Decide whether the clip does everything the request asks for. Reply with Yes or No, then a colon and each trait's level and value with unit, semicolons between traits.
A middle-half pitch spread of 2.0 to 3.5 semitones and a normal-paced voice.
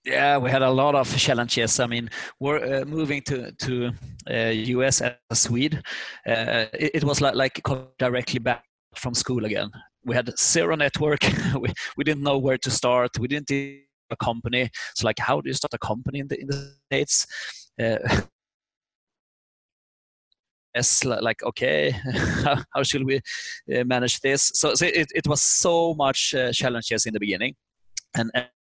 Yes: average, 2.8 semitones; average, 175 wpm